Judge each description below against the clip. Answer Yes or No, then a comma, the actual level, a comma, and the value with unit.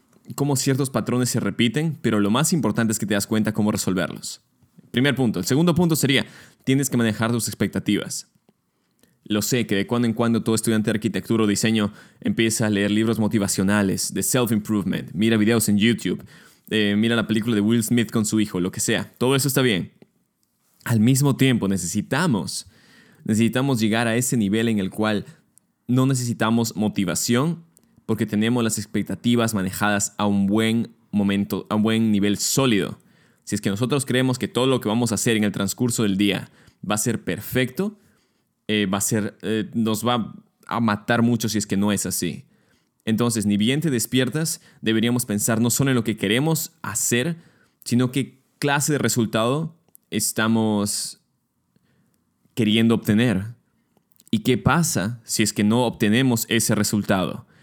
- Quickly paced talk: No, average, 175 wpm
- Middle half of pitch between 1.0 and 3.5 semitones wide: Yes, average, 3.0 semitones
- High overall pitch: No, low, 115 Hz